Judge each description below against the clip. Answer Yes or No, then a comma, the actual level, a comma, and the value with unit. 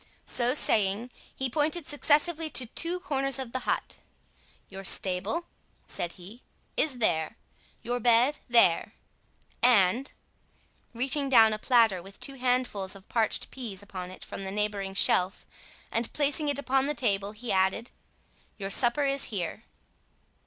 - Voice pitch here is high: Yes, high, 235 Hz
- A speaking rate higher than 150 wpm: No, average, 140 wpm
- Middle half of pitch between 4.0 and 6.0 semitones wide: Yes, wide, 5.6 semitones